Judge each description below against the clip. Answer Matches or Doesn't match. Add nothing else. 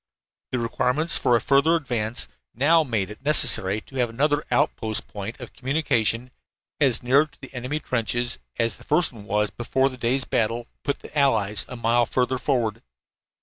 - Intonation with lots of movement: Doesn't match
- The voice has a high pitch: Doesn't match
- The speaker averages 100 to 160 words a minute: Doesn't match